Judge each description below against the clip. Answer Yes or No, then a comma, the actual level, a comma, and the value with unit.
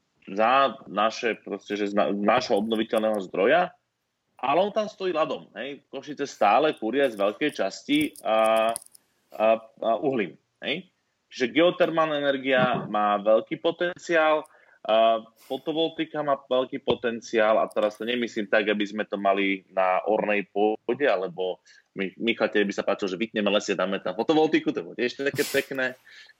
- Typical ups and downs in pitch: No, wide, 6.0 semitones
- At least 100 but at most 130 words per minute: No, average, 150 wpm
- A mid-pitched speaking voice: No, low, 115 Hz